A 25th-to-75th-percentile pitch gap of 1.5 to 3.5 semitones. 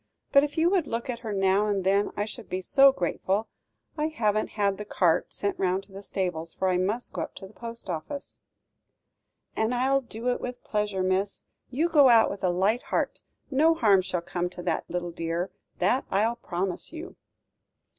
No: average, 4.8 semitones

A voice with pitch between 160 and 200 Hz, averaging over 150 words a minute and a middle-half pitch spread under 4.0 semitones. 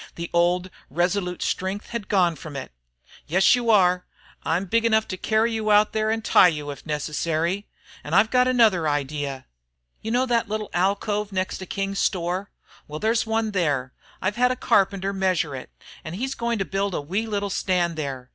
No: high, 190 Hz; average, 190 wpm; average, 4.3 semitones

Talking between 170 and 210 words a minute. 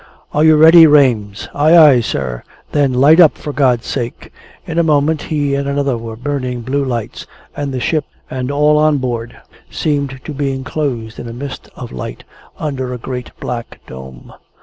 Yes: average, 180 wpm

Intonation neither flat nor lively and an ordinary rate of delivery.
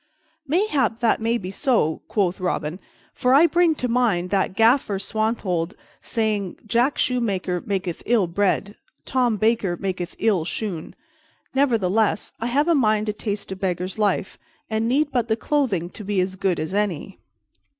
Yes: average, 4.2 semitones; average, 160 wpm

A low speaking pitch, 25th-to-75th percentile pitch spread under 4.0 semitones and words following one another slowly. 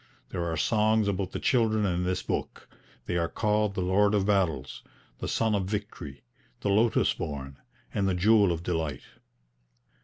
No: low, 100 Hz; average, 3.5 semitones; average, 165 wpm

